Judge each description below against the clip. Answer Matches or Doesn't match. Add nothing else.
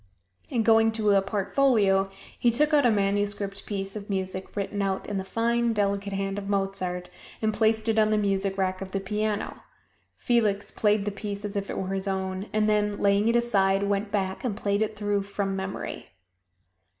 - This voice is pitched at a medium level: Doesn't match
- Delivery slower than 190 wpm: Doesn't match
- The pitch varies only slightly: Matches